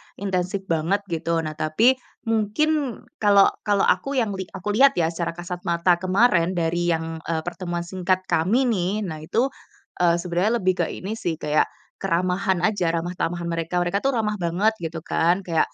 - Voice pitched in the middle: Yes, medium, 180 Hz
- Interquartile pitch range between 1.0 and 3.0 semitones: No, average, 3.4 semitones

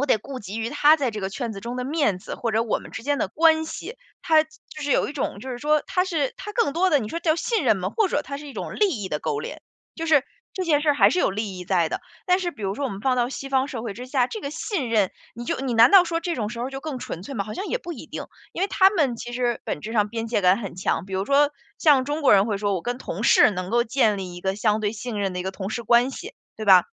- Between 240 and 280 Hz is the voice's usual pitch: Yes, high, 245 Hz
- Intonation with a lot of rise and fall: Yes, wide, 6.5 semitones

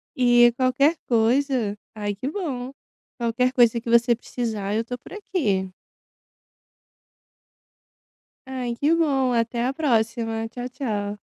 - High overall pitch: Yes, high, 240 Hz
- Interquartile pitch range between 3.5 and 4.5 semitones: No, narrow, 2.6 semitones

